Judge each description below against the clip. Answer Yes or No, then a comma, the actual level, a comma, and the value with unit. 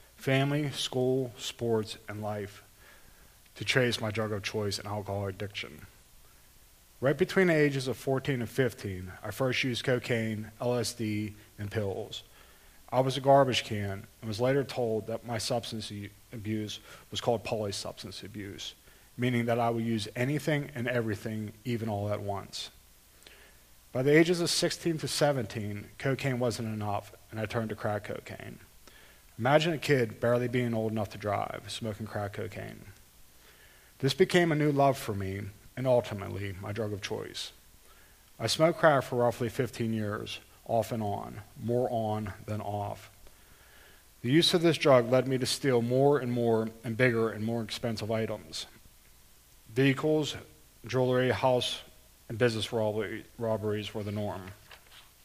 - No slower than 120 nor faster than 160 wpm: Yes, average, 150 wpm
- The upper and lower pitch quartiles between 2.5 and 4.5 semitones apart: Yes, average, 3.4 semitones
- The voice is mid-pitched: No, low, 115 Hz